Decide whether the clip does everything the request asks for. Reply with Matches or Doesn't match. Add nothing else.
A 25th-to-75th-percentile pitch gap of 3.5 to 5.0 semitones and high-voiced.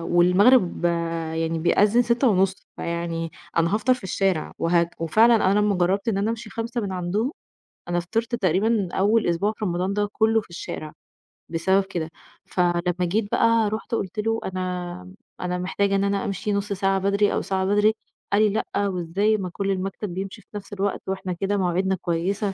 Doesn't match